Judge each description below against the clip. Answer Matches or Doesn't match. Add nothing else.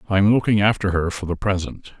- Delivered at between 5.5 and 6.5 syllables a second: Matches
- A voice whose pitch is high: Doesn't match